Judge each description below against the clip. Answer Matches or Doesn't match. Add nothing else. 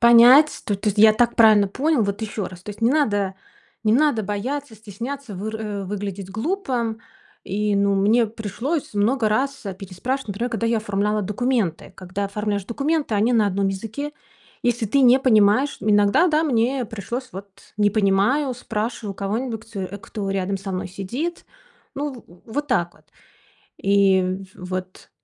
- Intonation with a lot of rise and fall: Doesn't match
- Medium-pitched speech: Doesn't match